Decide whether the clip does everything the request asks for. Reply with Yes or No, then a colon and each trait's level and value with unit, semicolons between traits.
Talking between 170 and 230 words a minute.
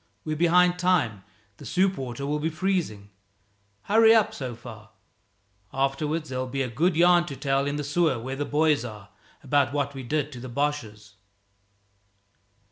No: average, 160 wpm